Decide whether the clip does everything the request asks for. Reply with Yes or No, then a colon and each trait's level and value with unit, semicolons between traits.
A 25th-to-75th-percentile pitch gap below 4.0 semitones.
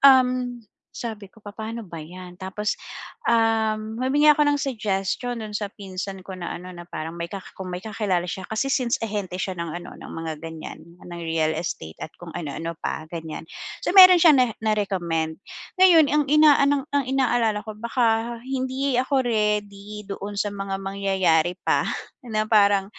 No: wide, 5.4 semitones